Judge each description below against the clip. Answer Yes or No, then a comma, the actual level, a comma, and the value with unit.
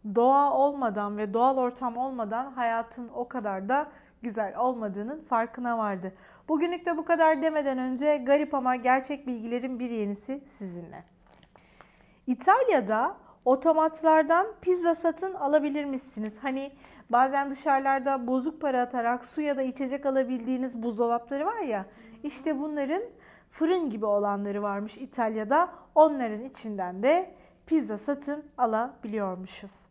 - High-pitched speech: Yes, very high, 255 Hz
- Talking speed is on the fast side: No, average, 120 wpm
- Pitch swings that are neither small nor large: Yes, average, 4.2 semitones